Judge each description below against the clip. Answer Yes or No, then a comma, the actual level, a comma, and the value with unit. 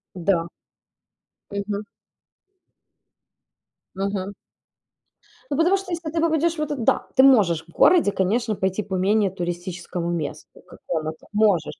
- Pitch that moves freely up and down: Yes, wide, 7.3 semitones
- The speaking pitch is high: Yes, high, 200 Hz